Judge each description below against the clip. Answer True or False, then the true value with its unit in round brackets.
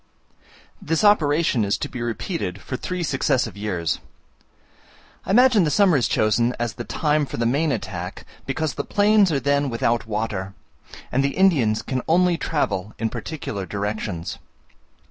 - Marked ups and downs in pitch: True (7.1 semitones)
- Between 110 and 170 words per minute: True (155 wpm)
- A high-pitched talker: False (130 Hz)